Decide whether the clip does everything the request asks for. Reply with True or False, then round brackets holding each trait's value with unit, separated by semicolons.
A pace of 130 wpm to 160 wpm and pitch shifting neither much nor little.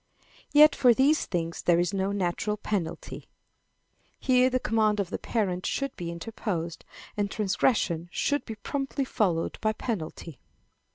False (140 wpm; 6.0 semitones)